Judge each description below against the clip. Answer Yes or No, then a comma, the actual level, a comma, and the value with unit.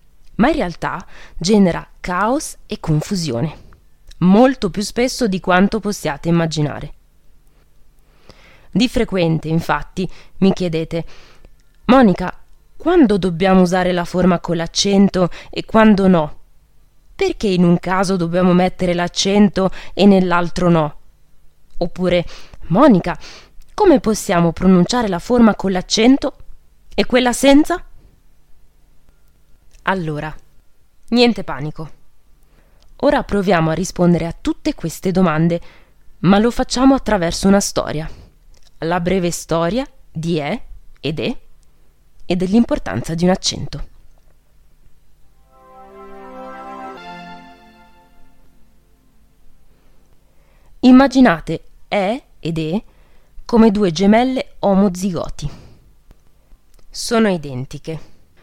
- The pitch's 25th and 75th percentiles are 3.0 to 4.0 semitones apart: No, average, 5.2 semitones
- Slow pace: Yes, slow, 95 wpm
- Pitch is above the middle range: No, medium, 180 Hz